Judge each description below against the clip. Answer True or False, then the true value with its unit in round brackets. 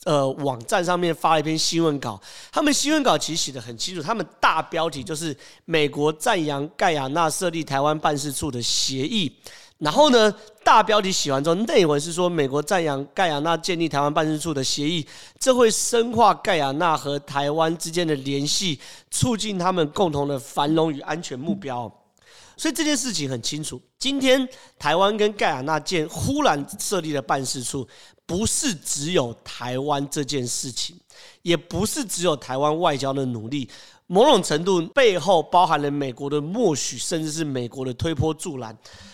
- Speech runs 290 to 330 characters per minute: False (275 characters per minute)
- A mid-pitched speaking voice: True (155 Hz)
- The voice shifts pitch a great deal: False (4.5 semitones)